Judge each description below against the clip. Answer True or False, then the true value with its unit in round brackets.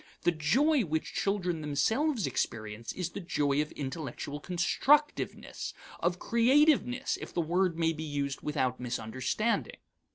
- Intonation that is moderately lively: False (7.6 semitones)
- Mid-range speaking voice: True (165 Hz)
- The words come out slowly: True (130 wpm)